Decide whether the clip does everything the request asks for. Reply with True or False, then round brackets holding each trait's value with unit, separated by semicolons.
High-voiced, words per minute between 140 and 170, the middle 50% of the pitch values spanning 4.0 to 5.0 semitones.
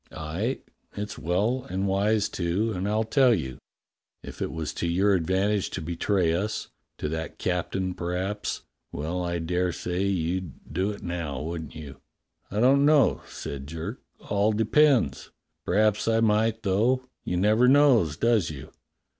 False (95 Hz; 160 wpm; 4.3 semitones)